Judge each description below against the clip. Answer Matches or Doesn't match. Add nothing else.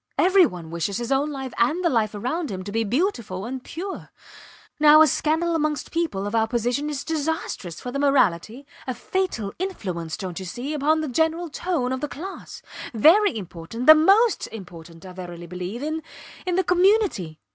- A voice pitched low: Doesn't match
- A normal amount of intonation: Doesn't match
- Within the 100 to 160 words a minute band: Doesn't match